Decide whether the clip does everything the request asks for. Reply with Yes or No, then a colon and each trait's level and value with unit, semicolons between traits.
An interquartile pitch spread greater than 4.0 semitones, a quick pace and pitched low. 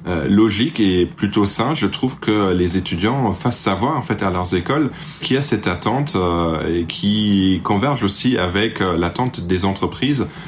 No: average, 5.1 semitones; average, 165 wpm; low, 100 Hz